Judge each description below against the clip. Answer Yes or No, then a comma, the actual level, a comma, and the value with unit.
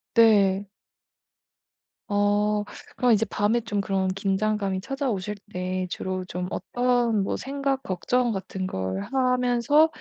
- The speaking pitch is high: Yes, high, 210 Hz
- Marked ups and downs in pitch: No, average, 4.4 semitones